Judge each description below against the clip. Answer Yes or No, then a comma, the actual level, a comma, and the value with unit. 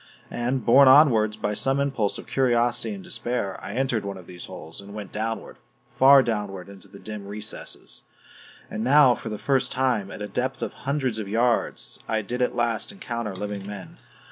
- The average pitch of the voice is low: Yes, low, 115 Hz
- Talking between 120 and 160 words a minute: No, average, 190 wpm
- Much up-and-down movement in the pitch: No, average, 4.0 semitones